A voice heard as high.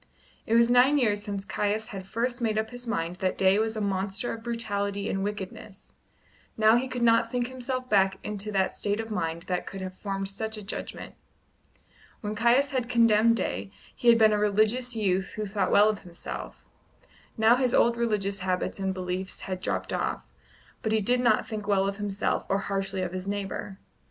Yes: high, 210 Hz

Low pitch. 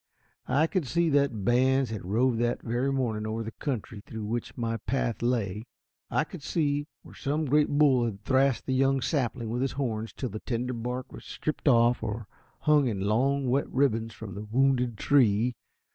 Yes: low, 125 Hz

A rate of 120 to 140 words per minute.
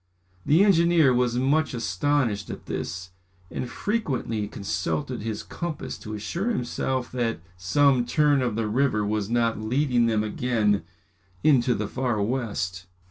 Yes: slow, 135 wpm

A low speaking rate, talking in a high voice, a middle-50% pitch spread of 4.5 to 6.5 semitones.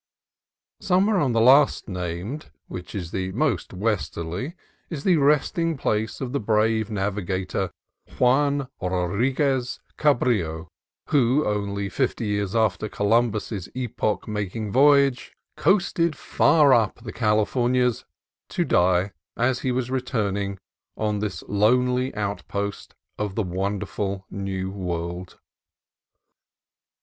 No: slow, 110 wpm; low, 110 Hz; average, 4.8 semitones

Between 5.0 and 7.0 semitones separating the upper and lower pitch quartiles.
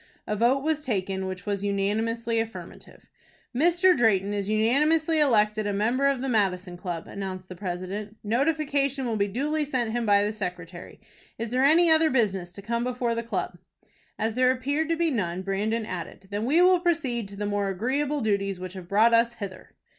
Yes: average, 5.3 semitones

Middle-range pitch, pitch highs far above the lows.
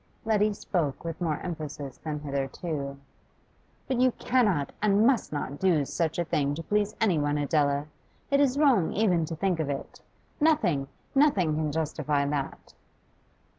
Yes: medium, 160 Hz; wide, 6.3 semitones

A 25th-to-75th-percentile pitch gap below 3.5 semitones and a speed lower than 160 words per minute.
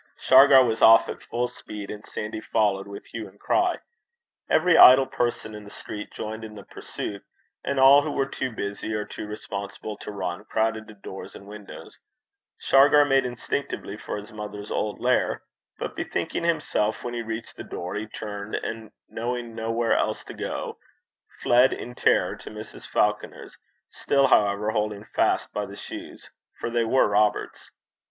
No: average, 2.8 semitones; average, 170 wpm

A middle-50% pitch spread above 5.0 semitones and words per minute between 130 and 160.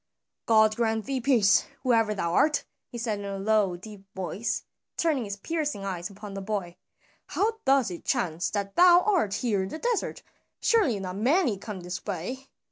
No: wide, 5.4 semitones; average, 180 wpm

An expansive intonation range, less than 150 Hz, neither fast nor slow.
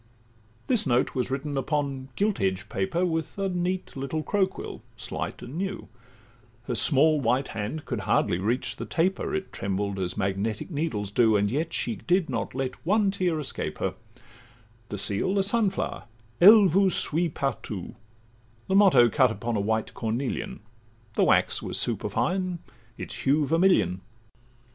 Yes: wide, 8.6 semitones; medium, 140 Hz; average, 160 wpm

